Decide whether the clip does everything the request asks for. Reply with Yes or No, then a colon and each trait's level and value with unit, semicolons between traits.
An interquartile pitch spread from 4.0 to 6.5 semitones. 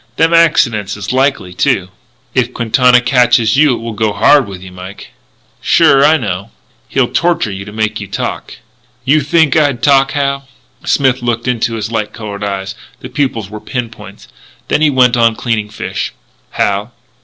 Yes: average, 4.6 semitones